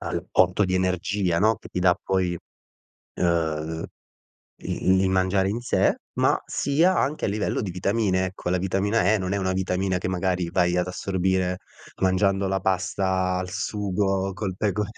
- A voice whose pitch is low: Yes, very low, 95 Hz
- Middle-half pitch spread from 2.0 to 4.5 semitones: No, narrow, 1.3 semitones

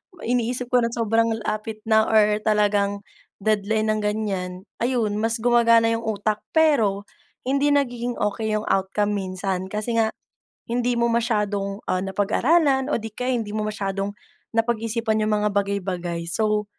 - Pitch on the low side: No, high, 215 Hz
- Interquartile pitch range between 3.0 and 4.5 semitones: No, narrow, 2.4 semitones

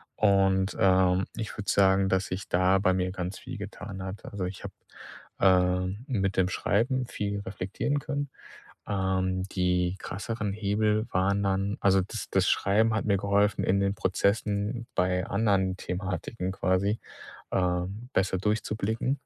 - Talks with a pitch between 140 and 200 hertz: No, low, 100 Hz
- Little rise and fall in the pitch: Yes, narrow, 2.1 semitones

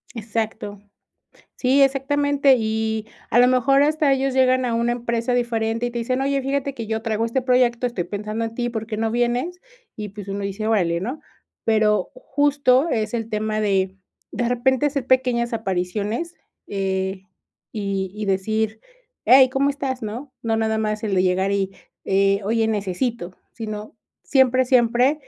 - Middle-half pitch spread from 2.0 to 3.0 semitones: No, average, 3.4 semitones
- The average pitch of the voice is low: No, high, 230 Hz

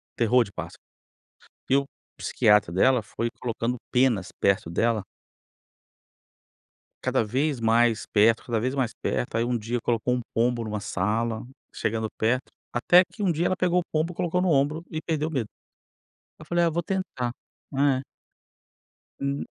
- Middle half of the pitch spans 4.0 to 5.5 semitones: Yes, average, 5.2 semitones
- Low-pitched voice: Yes, low, 125 Hz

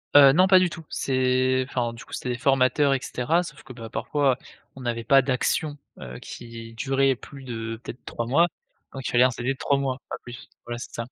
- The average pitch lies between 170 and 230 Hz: No, low, 130 Hz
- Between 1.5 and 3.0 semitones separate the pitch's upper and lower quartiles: Yes, narrow, 2.5 semitones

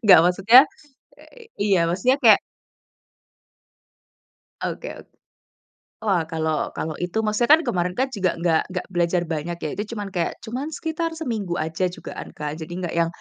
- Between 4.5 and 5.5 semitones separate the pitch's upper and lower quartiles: Yes, average, 5.1 semitones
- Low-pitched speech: No, medium, 185 Hz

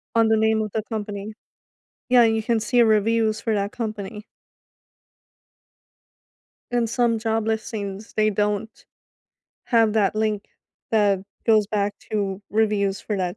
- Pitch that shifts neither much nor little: No, narrow, 1.4 semitones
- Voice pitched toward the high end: Yes, high, 215 Hz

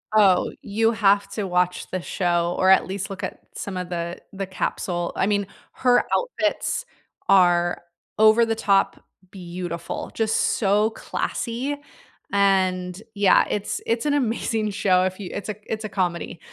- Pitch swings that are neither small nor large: Yes, average, 3.0 semitones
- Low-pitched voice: No, high, 195 Hz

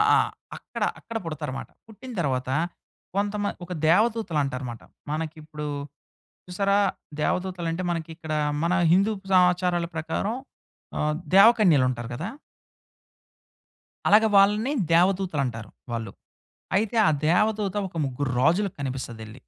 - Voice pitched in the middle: Yes, medium, 175 Hz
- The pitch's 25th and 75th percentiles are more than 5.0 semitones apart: Yes, wide, 5.4 semitones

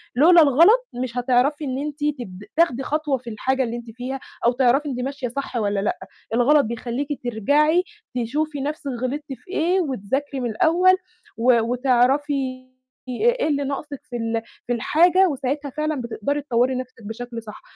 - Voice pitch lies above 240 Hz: Yes, very high, 265 Hz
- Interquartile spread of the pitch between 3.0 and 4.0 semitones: Yes, average, 3.6 semitones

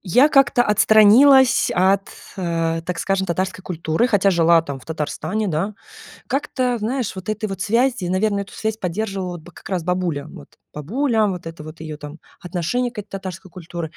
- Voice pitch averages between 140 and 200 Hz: Yes, high, 190 Hz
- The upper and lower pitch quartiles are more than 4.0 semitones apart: Yes, average, 4.4 semitones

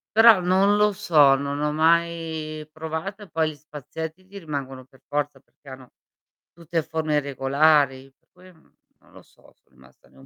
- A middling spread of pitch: Yes, average, 3.1 semitones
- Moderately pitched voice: Yes, medium, 155 Hz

